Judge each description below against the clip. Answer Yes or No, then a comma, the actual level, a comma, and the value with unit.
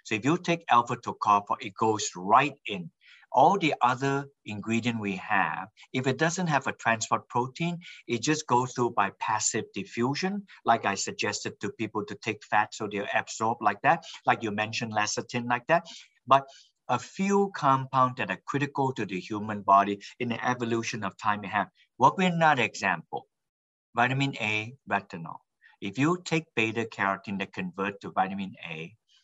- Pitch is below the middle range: Yes, low, 115 Hz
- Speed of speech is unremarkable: Yes, average, 175 wpm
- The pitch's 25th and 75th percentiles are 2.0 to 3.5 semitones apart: No, average, 4.6 semitones